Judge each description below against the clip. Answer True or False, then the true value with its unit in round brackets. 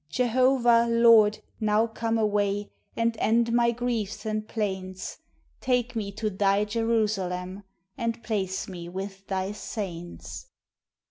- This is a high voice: True (215 Hz)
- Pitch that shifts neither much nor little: True (3.0 semitones)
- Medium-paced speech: False (120 wpm)